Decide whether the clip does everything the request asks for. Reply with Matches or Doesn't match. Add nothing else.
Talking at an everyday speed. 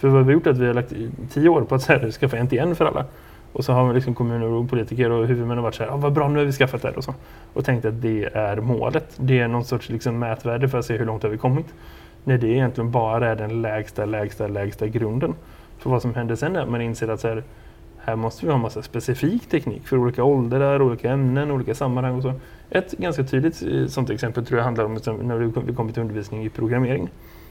Doesn't match